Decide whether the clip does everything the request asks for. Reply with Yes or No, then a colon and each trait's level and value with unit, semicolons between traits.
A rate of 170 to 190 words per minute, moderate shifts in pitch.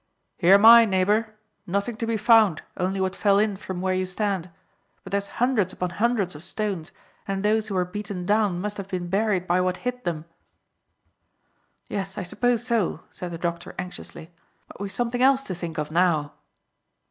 Yes: average, 185 wpm; average, 3.2 semitones